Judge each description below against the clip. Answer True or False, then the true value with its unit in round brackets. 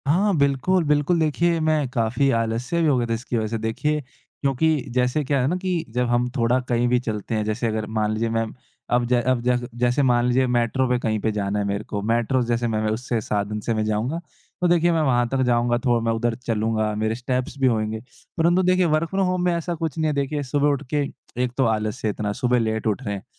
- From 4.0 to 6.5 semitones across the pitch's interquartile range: True (4.6 semitones)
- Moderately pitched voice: False (125 Hz)